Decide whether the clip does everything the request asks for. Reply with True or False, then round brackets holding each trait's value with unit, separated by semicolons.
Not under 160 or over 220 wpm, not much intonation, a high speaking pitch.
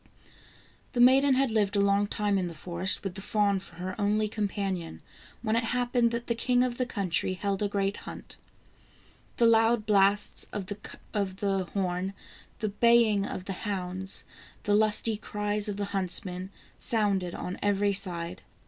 True (165 wpm; 2.3 semitones; 205 Hz)